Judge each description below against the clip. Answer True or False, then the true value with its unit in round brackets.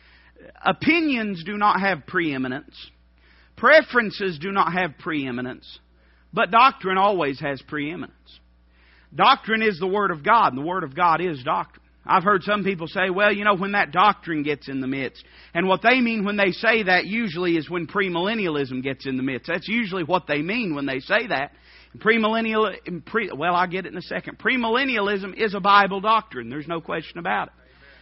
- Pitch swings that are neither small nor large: False (6.7 semitones)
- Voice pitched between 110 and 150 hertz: False (185 Hz)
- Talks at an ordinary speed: True (190 wpm)